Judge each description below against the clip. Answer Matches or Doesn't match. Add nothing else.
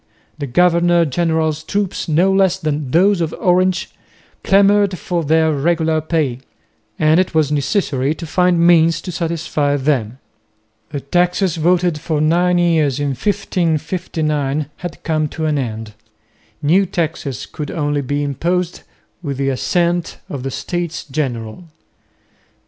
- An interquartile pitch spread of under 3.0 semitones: Doesn't match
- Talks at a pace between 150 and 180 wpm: Doesn't match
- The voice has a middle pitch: Matches